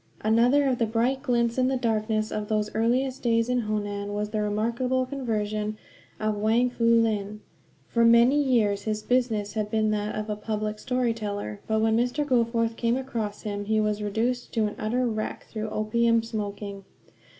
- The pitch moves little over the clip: Yes, narrow, 2.2 semitones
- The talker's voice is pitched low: No, high, 220 Hz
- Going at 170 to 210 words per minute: Yes, average, 180 wpm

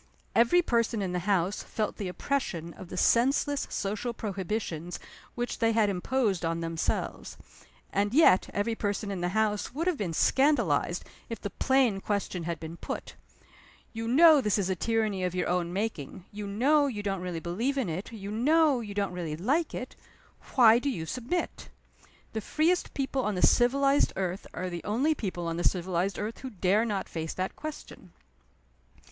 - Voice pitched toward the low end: No, high, 205 Hz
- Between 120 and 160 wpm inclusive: No, average, 180 wpm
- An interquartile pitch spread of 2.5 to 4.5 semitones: No, wide, 5.4 semitones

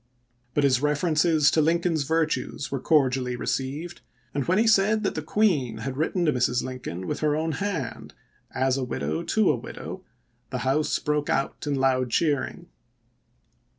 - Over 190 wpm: No, average, 175 wpm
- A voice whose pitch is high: No, medium, 145 Hz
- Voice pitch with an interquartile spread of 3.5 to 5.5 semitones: Yes, average, 3.8 semitones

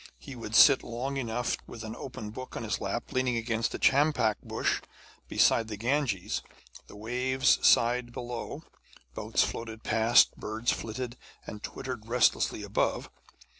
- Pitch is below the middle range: Yes, low, 120 Hz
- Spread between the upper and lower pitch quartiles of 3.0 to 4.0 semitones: No, narrow, 2.5 semitones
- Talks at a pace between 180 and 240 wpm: No, average, 145 wpm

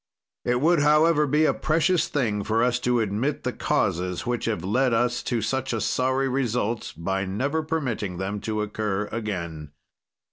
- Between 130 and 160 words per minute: No, average, 170 wpm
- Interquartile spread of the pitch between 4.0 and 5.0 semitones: Yes, average, 4.7 semitones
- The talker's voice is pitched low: Yes, low, 120 Hz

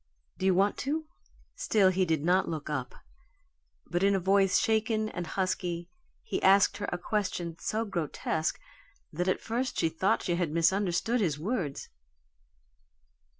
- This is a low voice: No, medium, 185 Hz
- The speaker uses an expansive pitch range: No, average, 3.5 semitones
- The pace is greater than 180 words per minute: No, average, 150 wpm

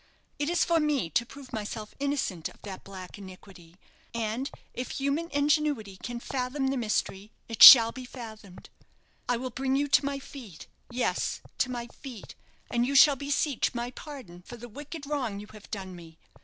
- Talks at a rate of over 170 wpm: Yes, average, 180 wpm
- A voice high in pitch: Yes, high, 245 Hz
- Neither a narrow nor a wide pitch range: Yes, average, 5.0 semitones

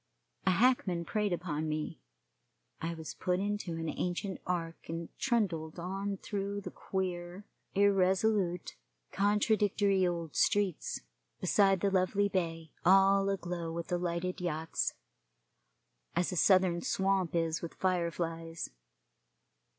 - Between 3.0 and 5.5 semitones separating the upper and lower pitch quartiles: No, narrow, 2.6 semitones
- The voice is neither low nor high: Yes, medium, 180 Hz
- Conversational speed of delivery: No, slow, 120 wpm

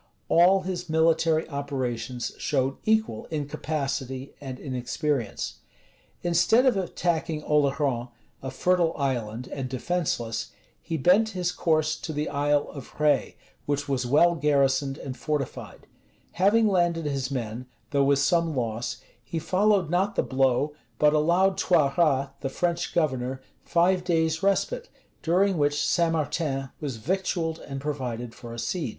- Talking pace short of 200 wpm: Yes, average, 140 wpm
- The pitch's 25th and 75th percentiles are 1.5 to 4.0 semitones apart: No, average, 4.4 semitones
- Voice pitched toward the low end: No, medium, 150 Hz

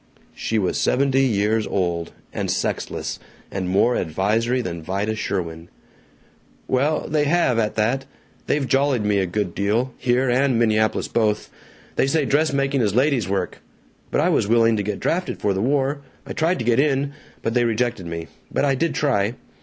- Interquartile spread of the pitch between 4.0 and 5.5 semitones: Yes, average, 5.1 semitones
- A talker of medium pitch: No, low, 115 Hz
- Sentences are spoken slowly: No, average, 175 wpm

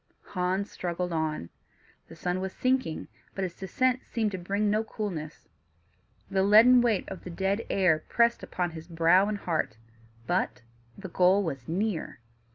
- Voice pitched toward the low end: No, high, 190 Hz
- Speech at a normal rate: Yes, average, 160 wpm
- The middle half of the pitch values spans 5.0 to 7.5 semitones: No, average, 3.7 semitones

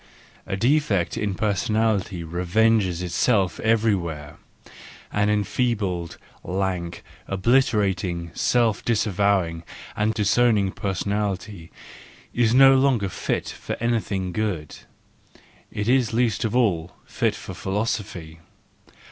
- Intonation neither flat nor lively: Yes, average, 3.8 semitones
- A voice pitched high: No, low, 100 Hz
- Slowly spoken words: Yes, slow, 95 wpm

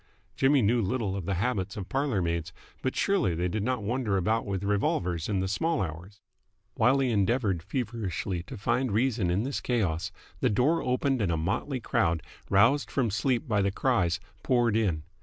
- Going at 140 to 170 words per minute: No, average, 185 wpm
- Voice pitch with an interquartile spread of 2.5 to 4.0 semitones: No, average, 5.2 semitones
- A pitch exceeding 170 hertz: No, low, 105 Hz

